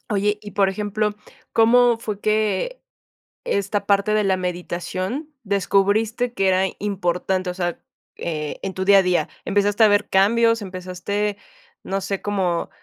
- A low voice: No, high, 200 Hz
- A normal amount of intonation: No, narrow, 2.2 semitones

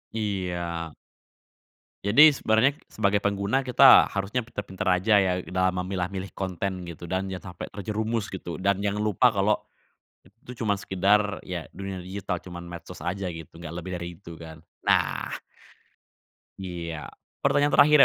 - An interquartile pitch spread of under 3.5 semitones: Yes, average, 2.9 semitones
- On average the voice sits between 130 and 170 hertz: No, very low, 95 Hz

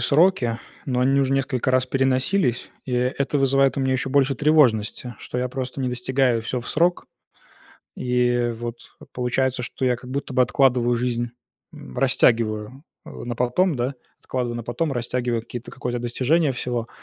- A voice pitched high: No, low, 125 Hz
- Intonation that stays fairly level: Yes, narrow, 1.9 semitones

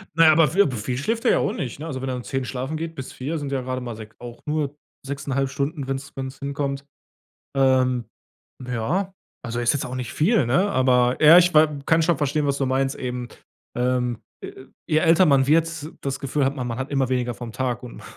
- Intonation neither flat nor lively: Yes, average, 3.2 semitones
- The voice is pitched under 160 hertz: Yes, low, 135 Hz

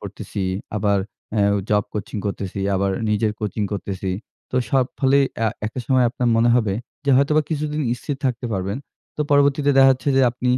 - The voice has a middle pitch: No, low, 120 Hz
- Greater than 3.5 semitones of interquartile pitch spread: Yes, average, 5.1 semitones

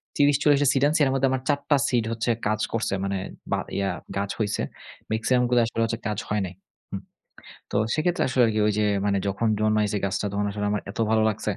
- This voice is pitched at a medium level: No, low, 110 Hz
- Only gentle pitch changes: No, average, 4.1 semitones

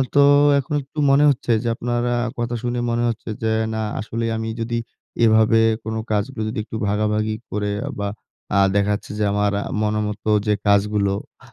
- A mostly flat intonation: Yes, narrow, 2.2 semitones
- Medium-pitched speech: No, low, 110 Hz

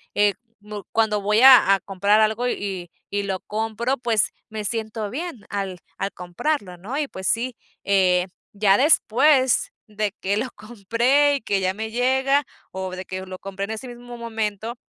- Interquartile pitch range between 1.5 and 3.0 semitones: No, average, 3.5 semitones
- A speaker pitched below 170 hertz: No, high, 215 Hz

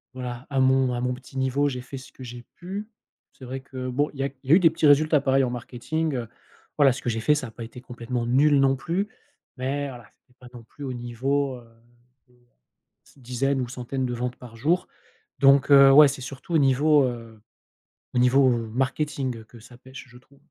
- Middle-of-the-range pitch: No, low, 130 Hz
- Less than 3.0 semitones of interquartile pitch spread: Yes, narrow, 2.4 semitones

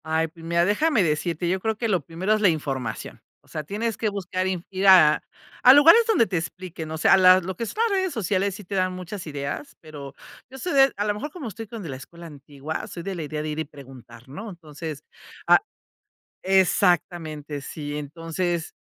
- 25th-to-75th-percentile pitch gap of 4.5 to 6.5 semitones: Yes, average, 4.9 semitones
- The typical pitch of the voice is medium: Yes, medium, 175 Hz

